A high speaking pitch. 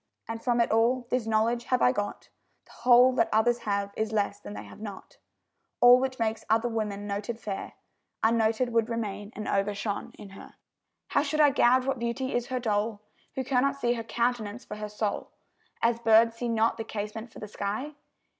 Yes: high, 225 Hz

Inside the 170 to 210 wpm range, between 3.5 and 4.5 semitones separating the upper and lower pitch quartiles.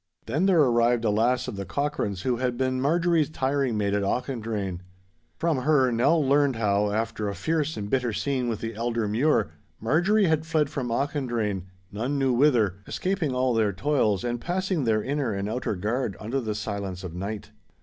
No: average, 180 wpm; average, 5.2 semitones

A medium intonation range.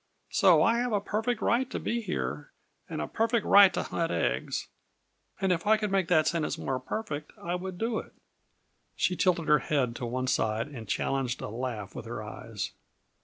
No: wide, 8.6 semitones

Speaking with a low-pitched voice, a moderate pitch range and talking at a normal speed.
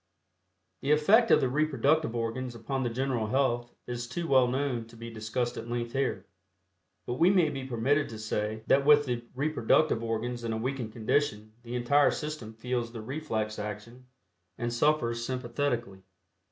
Yes: low, 120 Hz; average, 3.3 semitones; average, 165 wpm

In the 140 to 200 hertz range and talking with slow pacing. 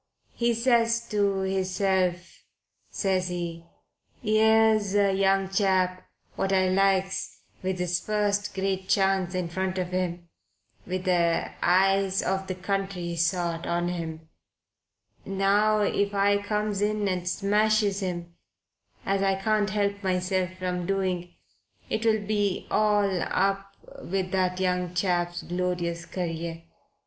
Yes: high, 190 Hz; slow, 125 wpm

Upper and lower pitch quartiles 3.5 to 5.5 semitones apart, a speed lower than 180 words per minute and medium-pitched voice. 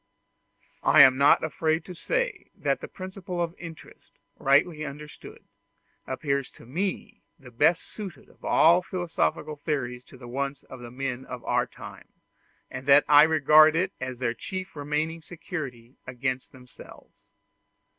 Yes: average, 4.2 semitones; average, 145 wpm; medium, 145 Hz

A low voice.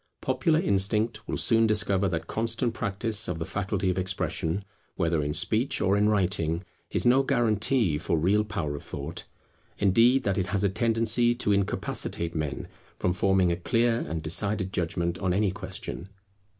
Yes: low, 100 Hz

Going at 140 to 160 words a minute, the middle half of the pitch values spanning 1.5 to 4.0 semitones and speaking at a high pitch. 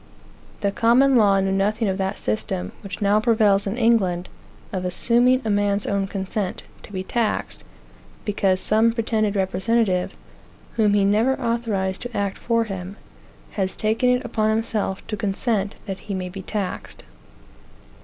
Yes: average, 155 wpm; average, 2.9 semitones; high, 205 Hz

